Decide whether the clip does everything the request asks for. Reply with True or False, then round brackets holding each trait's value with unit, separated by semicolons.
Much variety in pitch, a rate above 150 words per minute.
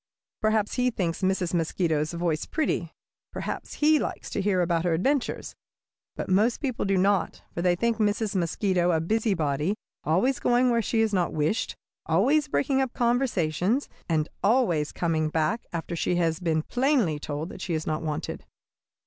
True (6.2 semitones; 165 wpm)